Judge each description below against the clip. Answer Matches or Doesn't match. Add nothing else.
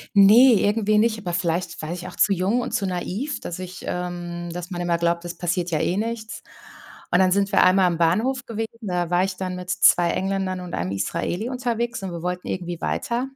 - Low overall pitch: Doesn't match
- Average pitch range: Matches